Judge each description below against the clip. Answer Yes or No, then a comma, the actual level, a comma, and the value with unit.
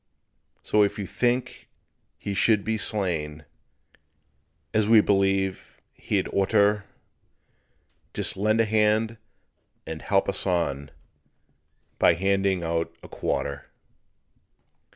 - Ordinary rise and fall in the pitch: Yes, average, 3.4 semitones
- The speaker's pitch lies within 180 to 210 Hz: No, low, 100 Hz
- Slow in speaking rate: Yes, slow, 105 wpm